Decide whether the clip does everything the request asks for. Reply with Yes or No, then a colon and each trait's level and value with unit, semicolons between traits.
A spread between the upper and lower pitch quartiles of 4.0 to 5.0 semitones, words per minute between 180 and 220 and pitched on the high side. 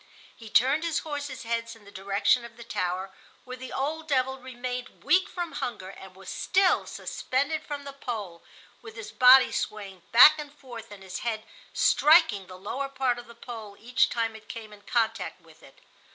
Yes: average, 4.5 semitones; average, 190 wpm; high, 235 Hz